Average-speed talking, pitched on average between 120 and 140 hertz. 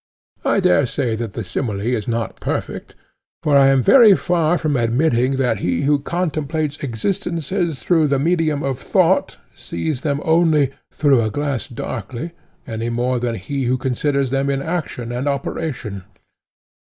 Yes: average, 155 wpm; low, 135 Hz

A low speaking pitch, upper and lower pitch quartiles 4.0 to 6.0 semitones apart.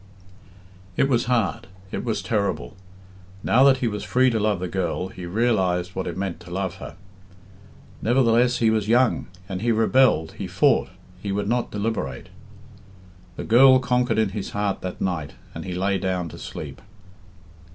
Yes: low, 105 Hz; average, 4.5 semitones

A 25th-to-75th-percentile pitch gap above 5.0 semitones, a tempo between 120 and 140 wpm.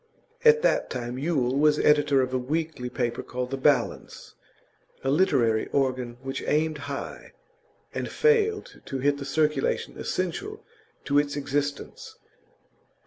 No: average, 3.1 semitones; slow, 135 wpm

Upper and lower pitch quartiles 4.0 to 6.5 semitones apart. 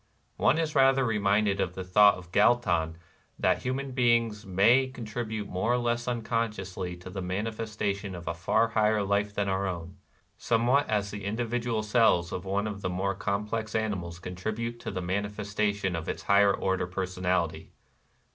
No: average, 3.5 semitones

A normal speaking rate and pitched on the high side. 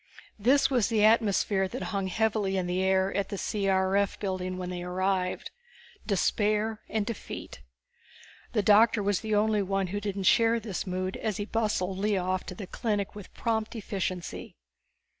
Yes: average, 165 wpm; high, 200 Hz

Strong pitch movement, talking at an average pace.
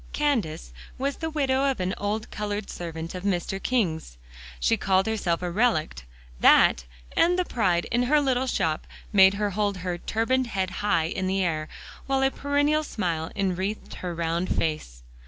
Yes: wide, 6.4 semitones; average, 170 wpm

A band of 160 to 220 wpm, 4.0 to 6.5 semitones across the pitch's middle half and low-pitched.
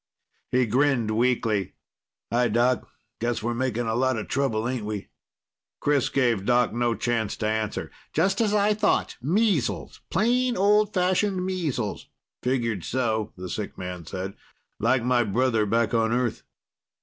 No: average, 150 wpm; average, 4.5 semitones; low, 120 Hz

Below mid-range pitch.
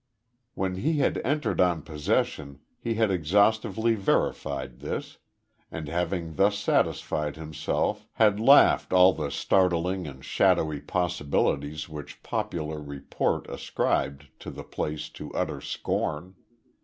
Yes: very low, 85 Hz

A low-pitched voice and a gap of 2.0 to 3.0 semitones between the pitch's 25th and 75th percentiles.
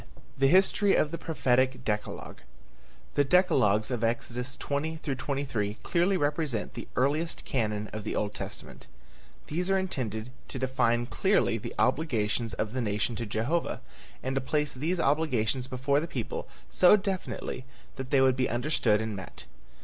No: low, 130 Hz; average, 5.1 semitones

